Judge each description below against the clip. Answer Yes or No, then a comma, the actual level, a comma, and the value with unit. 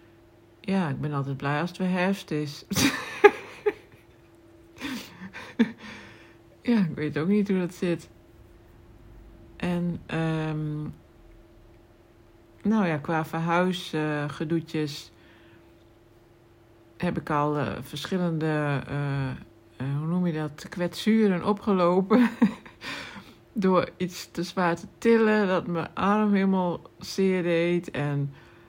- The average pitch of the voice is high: No, medium, 155 Hz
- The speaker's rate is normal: No, slow, 105 wpm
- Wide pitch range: Yes, wide, 8.1 semitones